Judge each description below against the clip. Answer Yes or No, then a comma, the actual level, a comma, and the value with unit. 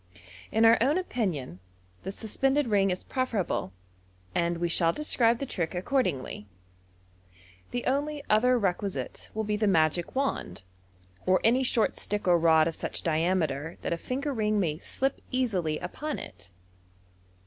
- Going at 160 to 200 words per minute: No, average, 150 wpm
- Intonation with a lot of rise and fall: Yes, wide, 7.1 semitones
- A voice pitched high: Yes, high, 205 Hz